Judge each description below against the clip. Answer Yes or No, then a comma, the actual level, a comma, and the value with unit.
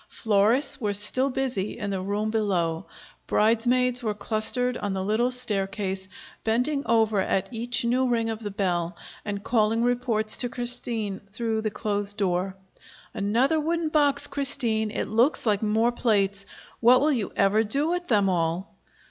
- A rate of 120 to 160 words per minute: Yes, average, 155 wpm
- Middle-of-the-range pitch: No, high, 220 Hz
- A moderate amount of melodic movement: Yes, average, 3.5 semitones